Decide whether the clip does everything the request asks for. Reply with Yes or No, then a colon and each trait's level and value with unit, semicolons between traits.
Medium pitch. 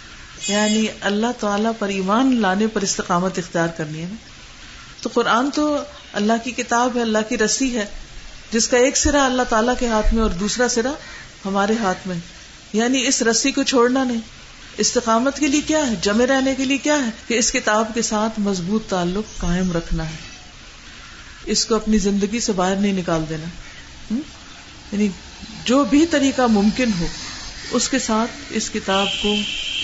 No: high, 220 Hz